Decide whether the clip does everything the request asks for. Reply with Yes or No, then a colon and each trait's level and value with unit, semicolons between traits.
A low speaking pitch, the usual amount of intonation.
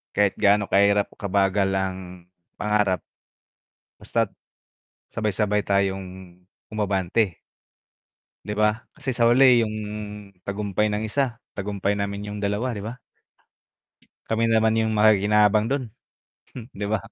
No: low, 105 Hz; narrow, 1.8 semitones